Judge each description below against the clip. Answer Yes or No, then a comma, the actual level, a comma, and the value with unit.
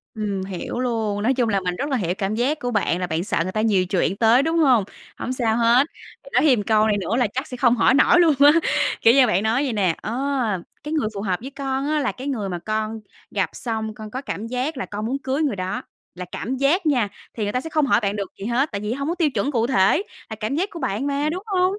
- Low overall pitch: No, high, 235 Hz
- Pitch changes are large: No, average, 5.0 semitones